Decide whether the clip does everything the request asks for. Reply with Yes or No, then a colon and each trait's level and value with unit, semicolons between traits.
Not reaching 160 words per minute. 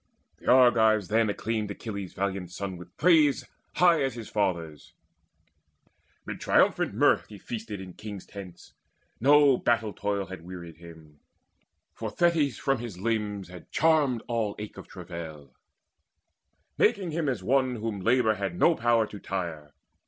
Yes: average, 145 wpm